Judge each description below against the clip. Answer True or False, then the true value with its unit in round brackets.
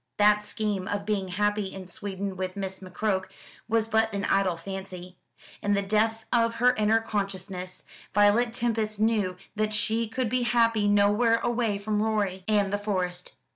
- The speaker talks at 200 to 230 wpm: False (165 wpm)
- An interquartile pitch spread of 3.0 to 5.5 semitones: False (2.4 semitones)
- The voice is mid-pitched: False (205 Hz)